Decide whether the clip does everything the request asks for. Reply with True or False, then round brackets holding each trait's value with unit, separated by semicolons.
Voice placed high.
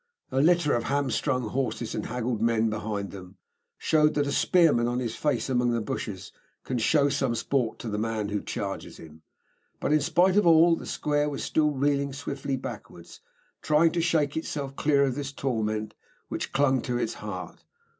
False (135 Hz)